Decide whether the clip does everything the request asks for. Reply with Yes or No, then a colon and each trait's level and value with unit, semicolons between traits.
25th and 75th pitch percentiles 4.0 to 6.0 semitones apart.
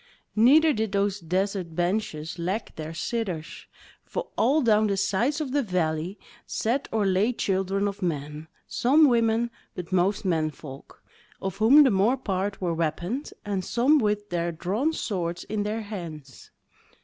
Yes: average, 4.6 semitones